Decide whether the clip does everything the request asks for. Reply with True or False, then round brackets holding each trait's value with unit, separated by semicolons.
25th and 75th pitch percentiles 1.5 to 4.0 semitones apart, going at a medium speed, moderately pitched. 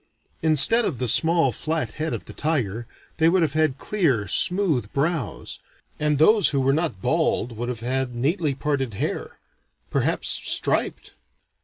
False (4.7 semitones; 155 wpm; 145 Hz)